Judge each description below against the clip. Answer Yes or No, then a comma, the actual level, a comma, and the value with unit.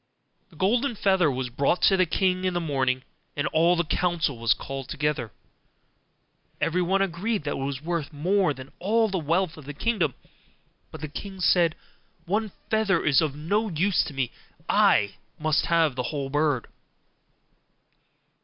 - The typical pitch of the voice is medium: Yes, medium, 165 Hz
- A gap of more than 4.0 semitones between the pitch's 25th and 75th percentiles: Yes, average, 5.0 semitones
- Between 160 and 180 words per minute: Yes, average, 165 wpm